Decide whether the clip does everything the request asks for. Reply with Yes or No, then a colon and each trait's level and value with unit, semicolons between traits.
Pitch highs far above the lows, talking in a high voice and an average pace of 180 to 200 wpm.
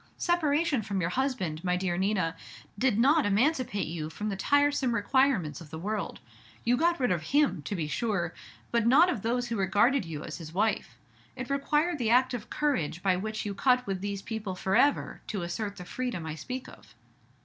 Yes: wide, 6.2 semitones; high, 215 Hz; average, 195 wpm